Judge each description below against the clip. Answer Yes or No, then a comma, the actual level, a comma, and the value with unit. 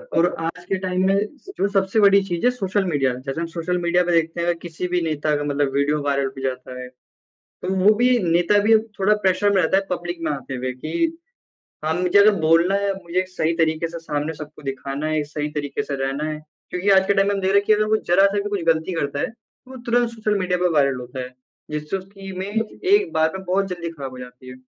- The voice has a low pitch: No, medium, 175 Hz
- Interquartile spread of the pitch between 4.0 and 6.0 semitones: Yes, average, 4.7 semitones